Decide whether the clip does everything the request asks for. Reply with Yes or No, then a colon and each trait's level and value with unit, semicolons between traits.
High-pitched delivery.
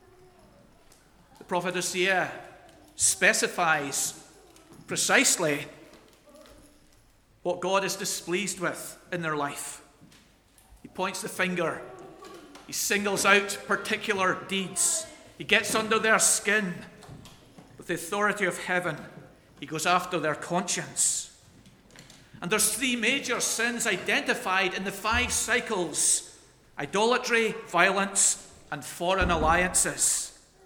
Yes: high, 195 Hz